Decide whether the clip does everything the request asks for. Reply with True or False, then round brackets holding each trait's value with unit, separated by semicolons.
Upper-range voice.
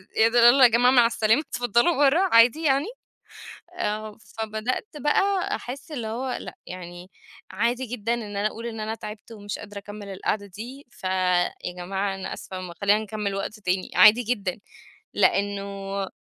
True (215 Hz)